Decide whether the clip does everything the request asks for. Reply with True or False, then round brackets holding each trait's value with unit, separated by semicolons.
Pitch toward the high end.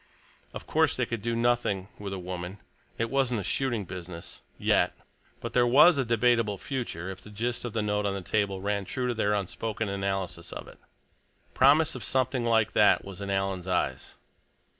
False (105 Hz)